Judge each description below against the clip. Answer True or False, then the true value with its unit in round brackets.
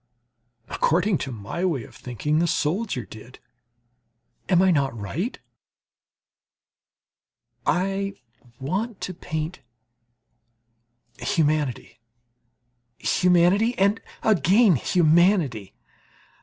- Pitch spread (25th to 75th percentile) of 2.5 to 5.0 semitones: False (5.6 semitones)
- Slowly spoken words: True (80 wpm)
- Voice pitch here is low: False (170 Hz)